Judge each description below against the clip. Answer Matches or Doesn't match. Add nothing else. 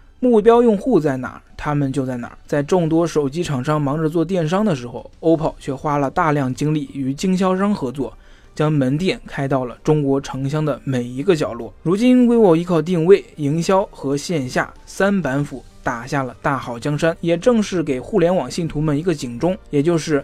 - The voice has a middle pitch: Matches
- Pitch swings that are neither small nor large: Matches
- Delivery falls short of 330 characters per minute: Matches